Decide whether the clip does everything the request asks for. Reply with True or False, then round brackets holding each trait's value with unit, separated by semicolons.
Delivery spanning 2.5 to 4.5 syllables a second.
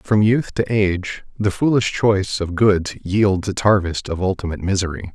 False (4.9 syllables/s)